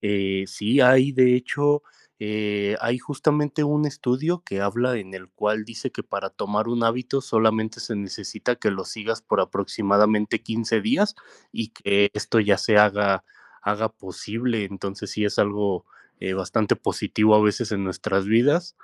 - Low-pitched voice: Yes, low, 110 Hz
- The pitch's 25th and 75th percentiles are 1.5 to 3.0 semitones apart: No, average, 3.6 semitones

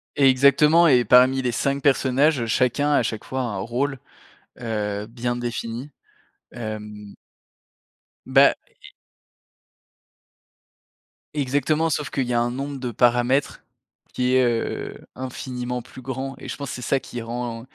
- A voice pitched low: Yes, low, 125 Hz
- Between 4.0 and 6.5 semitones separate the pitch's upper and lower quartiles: No, narrow, 2.4 semitones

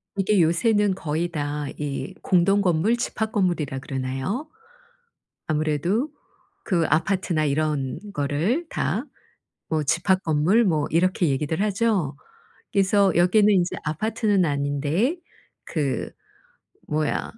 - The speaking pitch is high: No, medium, 170 Hz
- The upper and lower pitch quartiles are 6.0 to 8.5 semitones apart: No, average, 5.2 semitones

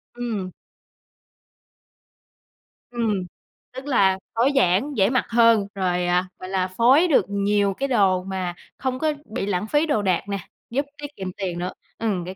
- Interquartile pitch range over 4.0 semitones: Yes, average, 5.2 semitones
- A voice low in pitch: No, high, 205 Hz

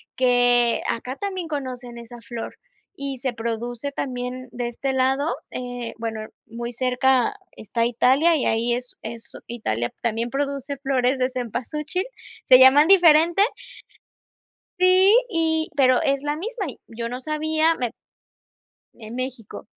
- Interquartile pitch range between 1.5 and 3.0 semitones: No, average, 3.6 semitones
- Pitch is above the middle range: Yes, very high, 255 Hz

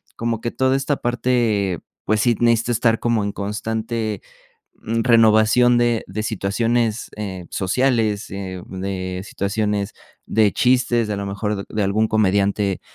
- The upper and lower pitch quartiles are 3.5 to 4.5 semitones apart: No, average, 2.9 semitones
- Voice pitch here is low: Yes, low, 110 Hz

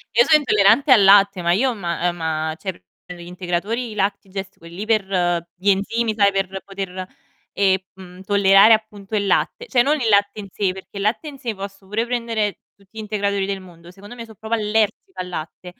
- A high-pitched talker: Yes, high, 200 Hz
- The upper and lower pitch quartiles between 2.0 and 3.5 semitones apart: Yes, narrow, 2.6 semitones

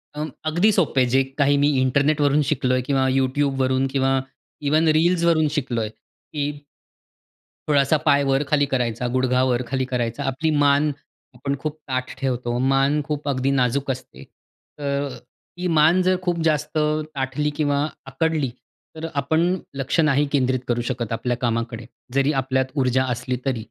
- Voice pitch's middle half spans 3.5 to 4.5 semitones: No, average, 2.8 semitones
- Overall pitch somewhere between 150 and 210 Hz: No, low, 135 Hz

